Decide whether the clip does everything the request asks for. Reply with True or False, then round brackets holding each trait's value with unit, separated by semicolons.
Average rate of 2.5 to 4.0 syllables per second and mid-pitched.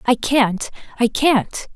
False (3.1 syllables/s; 240 Hz)